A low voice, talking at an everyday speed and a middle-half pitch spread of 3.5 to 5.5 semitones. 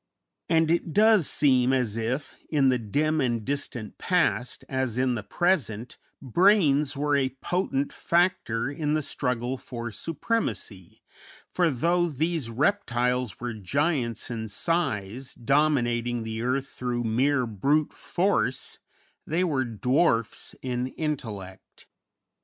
No: low, 130 Hz; slow, 125 wpm; average, 4.7 semitones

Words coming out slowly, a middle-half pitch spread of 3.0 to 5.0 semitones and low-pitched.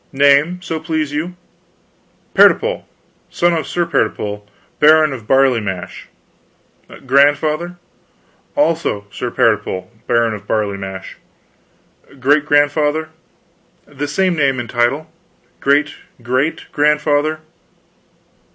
No: slow, 100 wpm; average, 4.6 semitones; medium, 145 Hz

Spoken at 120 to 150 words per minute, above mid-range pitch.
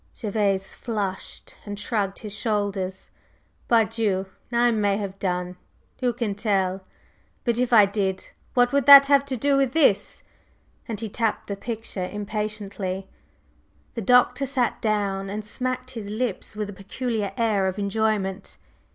Yes: average, 145 wpm; high, 210 Hz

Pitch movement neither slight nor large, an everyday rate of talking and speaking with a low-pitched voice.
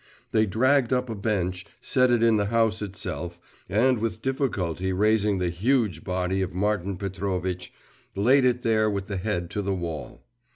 Yes: average, 3.8 semitones; average, 170 wpm; low, 100 Hz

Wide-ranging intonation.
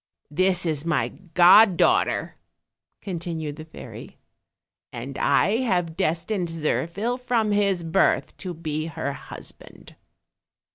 No: average, 3.7 semitones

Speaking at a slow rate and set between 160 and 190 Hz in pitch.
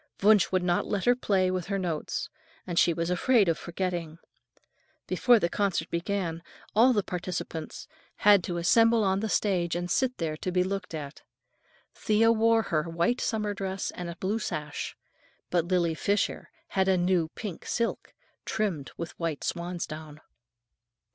No: average, 160 wpm; medium, 185 Hz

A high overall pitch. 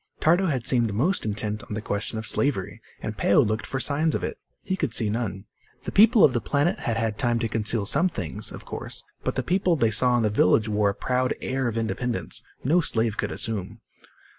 No: low, 115 Hz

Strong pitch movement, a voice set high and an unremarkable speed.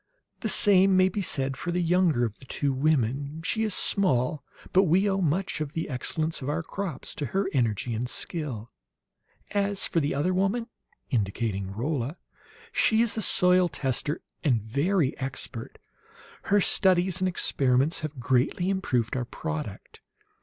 No: wide, 6.3 semitones; medium, 155 Hz; average, 160 wpm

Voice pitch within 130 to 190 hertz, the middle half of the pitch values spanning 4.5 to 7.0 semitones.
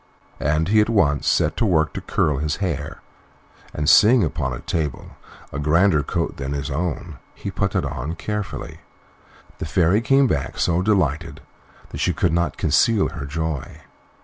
No: very low, 80 Hz; average, 4.8 semitones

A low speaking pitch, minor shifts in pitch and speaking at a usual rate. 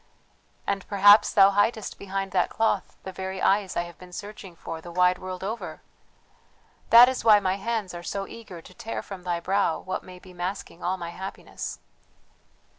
No: high, 190 Hz; narrow, 2.0 semitones; average, 185 wpm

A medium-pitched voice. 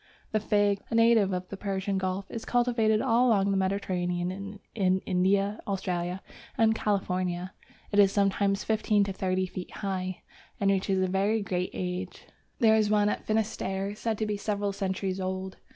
No: high, 195 Hz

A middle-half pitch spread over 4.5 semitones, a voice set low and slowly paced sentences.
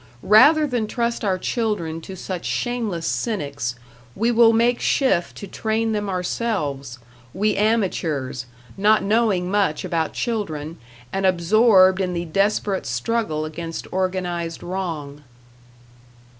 No: average, 4.9 semitones; high, 190 Hz; slow, 120 wpm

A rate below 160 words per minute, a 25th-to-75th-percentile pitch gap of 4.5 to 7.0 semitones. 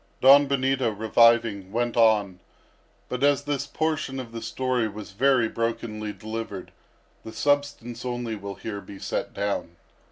No: average, 140 wpm; average, 3.6 semitones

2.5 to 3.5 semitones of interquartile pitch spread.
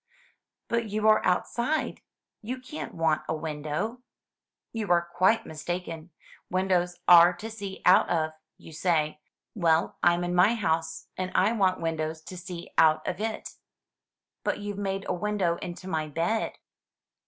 No: average, 4.0 semitones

